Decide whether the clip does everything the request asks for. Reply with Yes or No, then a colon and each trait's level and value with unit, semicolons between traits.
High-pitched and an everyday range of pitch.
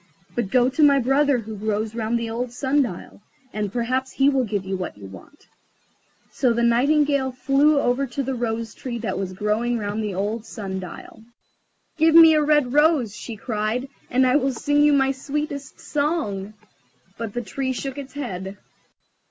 Yes: high, 245 Hz; average, 4.4 semitones